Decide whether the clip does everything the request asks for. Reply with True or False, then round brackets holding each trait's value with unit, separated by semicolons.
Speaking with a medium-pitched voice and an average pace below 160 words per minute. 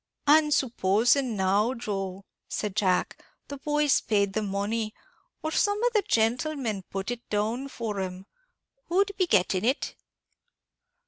False (225 Hz; 135 wpm)